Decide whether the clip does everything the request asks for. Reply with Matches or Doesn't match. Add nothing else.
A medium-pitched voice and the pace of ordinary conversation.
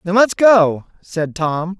Matches